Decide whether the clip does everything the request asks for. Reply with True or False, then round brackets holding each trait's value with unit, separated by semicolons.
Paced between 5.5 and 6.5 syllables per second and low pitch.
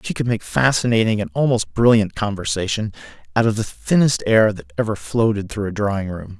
True (5.6 syllables/s; 105 Hz)